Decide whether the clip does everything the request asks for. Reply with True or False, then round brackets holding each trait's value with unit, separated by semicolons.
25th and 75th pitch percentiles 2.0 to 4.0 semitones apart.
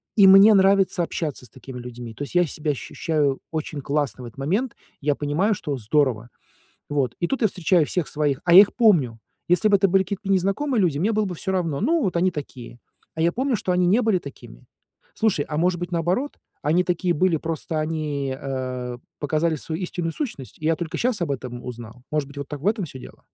False (5.3 semitones)